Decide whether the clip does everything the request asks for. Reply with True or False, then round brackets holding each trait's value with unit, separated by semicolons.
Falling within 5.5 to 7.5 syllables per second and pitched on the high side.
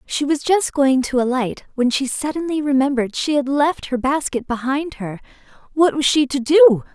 False (4.9 syllables/s; 275 Hz)